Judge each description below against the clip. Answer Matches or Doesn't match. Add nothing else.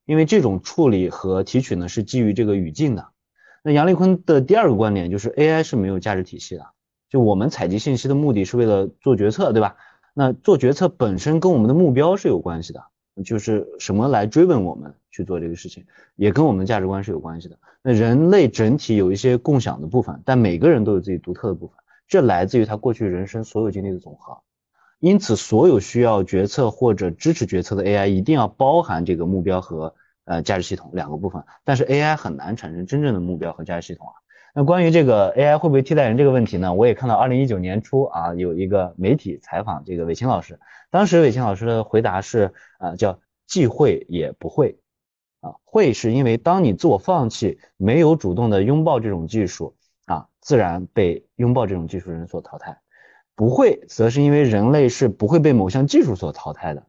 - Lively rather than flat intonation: Matches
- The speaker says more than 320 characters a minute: Matches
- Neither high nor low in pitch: Doesn't match